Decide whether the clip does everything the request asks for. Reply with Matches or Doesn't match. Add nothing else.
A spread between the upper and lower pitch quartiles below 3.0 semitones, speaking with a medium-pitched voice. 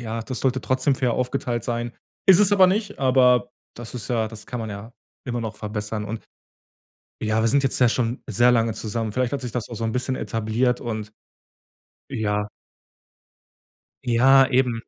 Doesn't match